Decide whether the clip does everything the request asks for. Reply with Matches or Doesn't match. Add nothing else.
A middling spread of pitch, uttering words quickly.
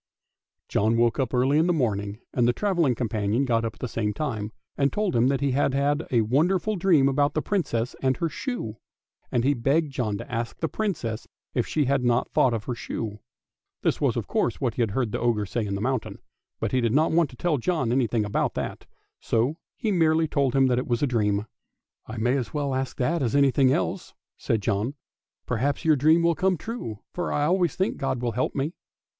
Matches